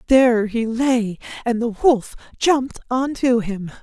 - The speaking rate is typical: Yes, average, 155 wpm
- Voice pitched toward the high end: Yes, high, 240 Hz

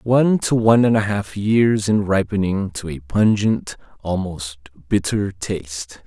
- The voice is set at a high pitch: No, low, 100 Hz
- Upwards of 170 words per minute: No, average, 150 wpm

